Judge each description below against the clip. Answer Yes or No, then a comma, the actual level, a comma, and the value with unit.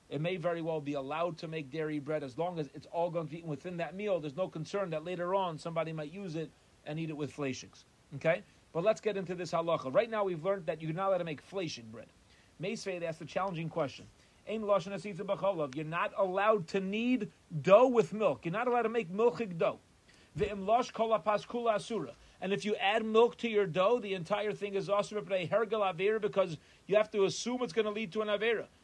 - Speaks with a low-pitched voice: No, high, 190 Hz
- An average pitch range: Yes, average, 4.6 semitones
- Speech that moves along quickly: Yes, fast, 210 wpm